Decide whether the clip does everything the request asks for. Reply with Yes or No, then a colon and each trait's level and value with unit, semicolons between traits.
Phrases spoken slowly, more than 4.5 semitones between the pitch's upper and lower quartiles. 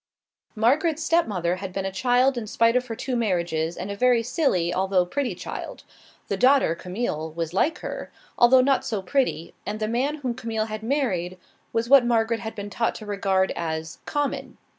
No: average, 185 wpm; average, 5.3 semitones